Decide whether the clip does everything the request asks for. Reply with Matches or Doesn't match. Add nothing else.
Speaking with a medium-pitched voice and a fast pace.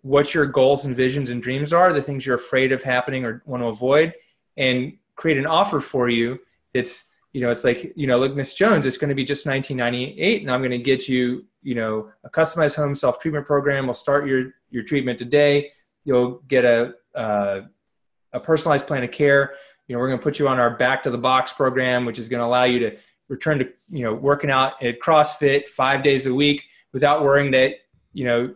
Doesn't match